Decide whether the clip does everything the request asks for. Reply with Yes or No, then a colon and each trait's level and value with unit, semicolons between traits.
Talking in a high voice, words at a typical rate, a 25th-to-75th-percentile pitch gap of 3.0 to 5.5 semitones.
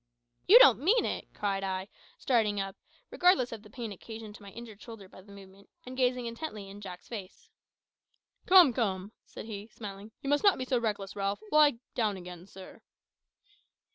Yes: high, 215 Hz; average, 180 wpm; average, 4.2 semitones